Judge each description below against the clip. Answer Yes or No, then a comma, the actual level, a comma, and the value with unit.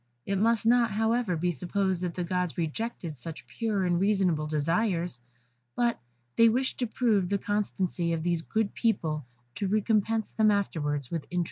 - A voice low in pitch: No, high, 190 Hz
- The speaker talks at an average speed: Yes, average, 165 wpm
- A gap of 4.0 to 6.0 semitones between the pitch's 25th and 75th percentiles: Yes, average, 4.7 semitones